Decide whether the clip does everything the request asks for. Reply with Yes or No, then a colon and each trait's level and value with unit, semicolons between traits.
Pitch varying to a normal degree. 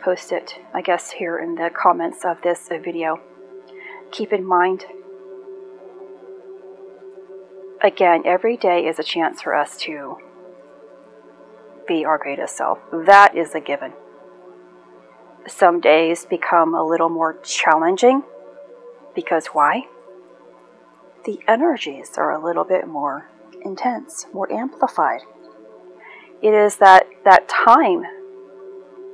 Yes: average, 3.9 semitones